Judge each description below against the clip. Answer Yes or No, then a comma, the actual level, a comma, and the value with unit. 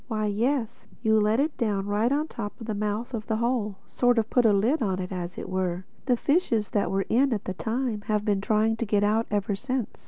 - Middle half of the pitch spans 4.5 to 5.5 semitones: No, average, 2.7 semitones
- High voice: Yes, high, 215 Hz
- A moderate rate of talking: No, fast, 240 wpm